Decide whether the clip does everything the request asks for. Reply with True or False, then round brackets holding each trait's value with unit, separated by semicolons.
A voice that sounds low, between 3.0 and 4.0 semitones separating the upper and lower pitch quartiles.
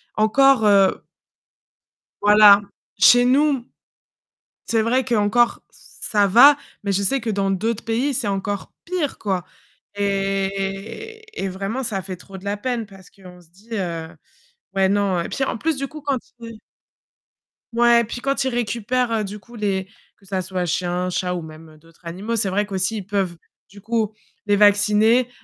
False (205 Hz; 3.5 semitones)